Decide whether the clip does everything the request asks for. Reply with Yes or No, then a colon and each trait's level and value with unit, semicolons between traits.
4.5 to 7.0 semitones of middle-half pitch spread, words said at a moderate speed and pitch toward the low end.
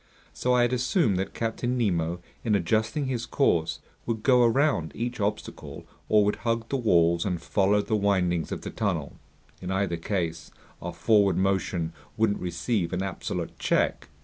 Yes: average, 4.8 semitones; average, 165 wpm; low, 100 Hz